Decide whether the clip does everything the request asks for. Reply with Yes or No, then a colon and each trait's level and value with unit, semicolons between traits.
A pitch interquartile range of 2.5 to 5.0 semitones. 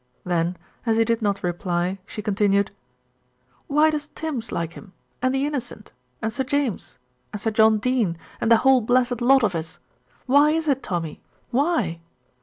No: wide, 5.4 semitones